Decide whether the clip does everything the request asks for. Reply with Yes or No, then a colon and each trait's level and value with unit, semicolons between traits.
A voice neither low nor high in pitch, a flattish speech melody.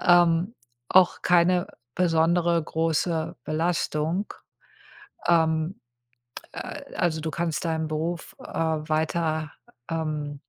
Yes: medium, 165 Hz; narrow, 1.6 semitones